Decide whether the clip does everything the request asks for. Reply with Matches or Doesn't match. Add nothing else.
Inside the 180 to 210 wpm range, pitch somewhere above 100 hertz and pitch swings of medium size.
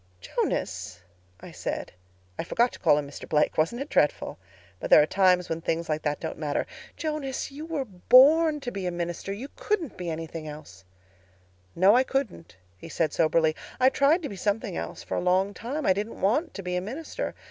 Doesn't match